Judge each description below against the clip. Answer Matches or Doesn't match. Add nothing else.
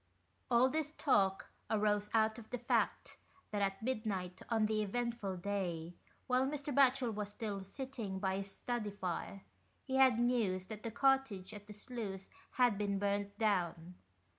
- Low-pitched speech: Doesn't match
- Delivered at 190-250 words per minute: Doesn't match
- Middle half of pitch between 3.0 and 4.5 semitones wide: Matches